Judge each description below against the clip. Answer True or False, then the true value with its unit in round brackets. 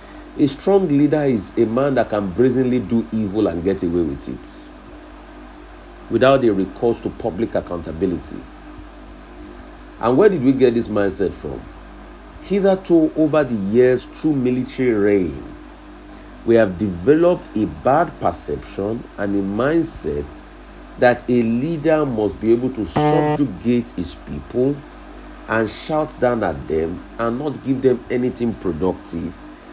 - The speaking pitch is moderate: False (125 Hz)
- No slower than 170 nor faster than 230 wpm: False (135 wpm)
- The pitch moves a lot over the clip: True (6.4 semitones)